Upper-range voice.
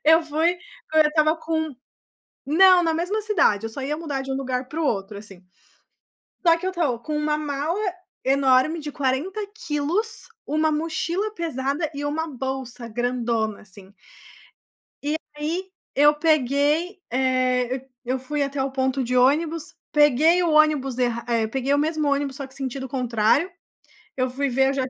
Yes: very high, 285 Hz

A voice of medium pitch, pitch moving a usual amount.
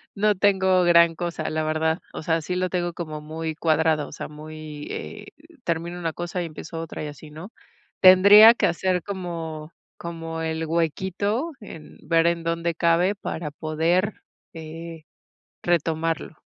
No: medium, 165 Hz; narrow, 2.2 semitones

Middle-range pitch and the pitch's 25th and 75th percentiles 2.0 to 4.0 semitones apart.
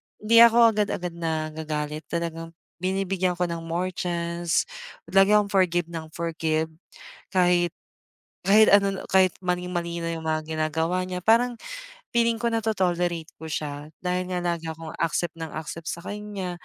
Yes: medium, 175 Hz; average, 2.8 semitones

